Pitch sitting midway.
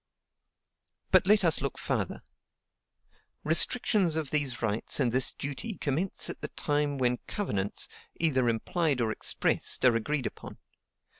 Yes: medium, 145 Hz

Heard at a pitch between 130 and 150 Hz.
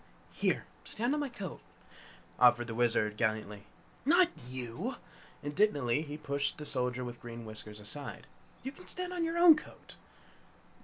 Yes: medium, 140 Hz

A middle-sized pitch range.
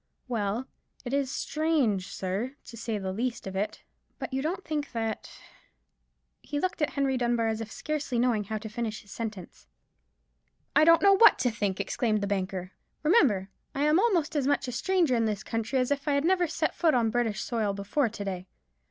No: wide, 5.7 semitones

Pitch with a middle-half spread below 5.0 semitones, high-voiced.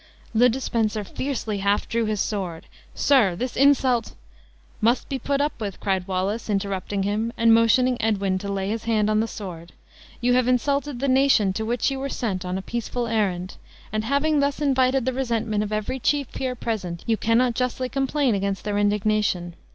Yes: average, 4.1 semitones; high, 225 Hz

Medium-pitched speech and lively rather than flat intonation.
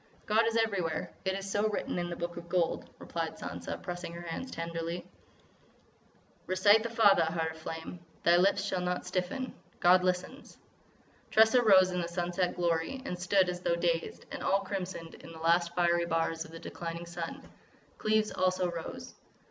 No: medium, 180 Hz; narrow, 2.5 semitones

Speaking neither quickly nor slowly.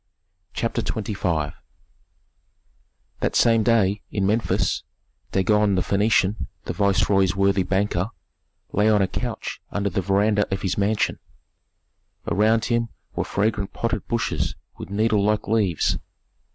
No: slow, 125 wpm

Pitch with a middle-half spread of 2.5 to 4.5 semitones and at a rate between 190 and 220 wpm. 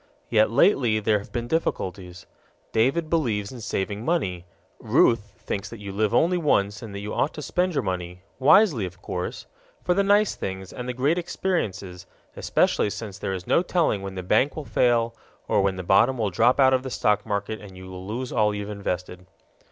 No: wide, 5.4 semitones; average, 200 wpm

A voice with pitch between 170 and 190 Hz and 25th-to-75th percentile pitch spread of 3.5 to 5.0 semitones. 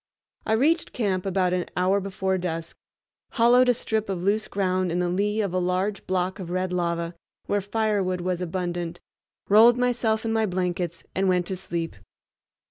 No: medium, 185 Hz; average, 2.9 semitones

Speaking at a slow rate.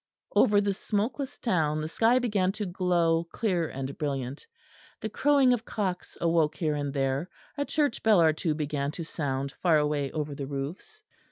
No: average, 175 wpm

